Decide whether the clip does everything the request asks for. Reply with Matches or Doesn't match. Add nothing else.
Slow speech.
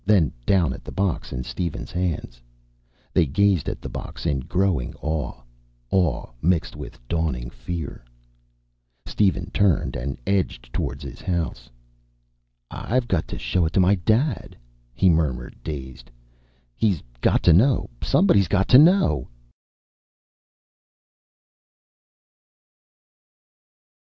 Matches